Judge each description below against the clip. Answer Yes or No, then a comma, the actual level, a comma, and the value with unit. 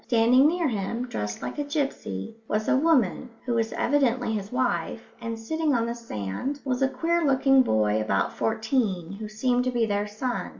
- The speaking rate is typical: Yes, average, 185 wpm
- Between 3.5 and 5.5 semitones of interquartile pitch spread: Yes, average, 4.2 semitones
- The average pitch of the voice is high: Yes, high, 235 Hz